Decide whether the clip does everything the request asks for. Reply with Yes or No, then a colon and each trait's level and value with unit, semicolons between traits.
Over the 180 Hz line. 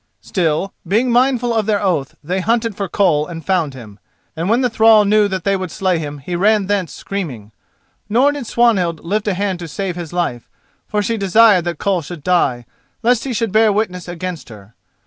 Yes: high, 190 Hz